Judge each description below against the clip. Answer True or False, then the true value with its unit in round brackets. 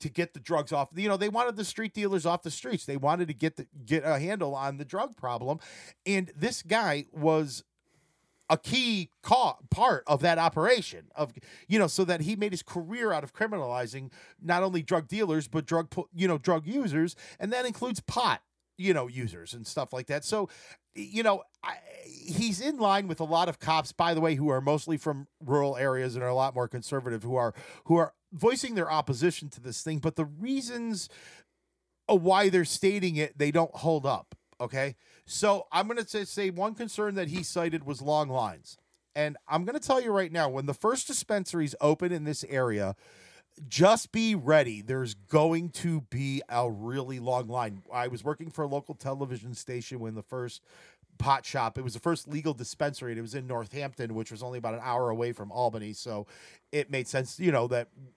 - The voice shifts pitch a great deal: True (5.9 semitones)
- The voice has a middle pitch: True (155 Hz)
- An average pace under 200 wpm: False (205 wpm)